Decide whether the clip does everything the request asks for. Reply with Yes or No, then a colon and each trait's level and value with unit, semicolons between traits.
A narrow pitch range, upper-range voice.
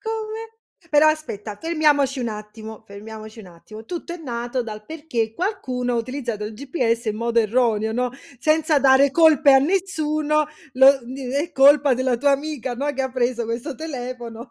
No: average, 4.8 semitones; very high, 260 Hz